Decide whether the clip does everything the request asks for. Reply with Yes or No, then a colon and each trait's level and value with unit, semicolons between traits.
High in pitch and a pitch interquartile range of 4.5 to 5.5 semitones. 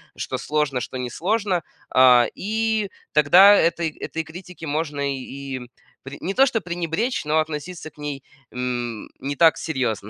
No: medium, 155 Hz; average, 5.1 semitones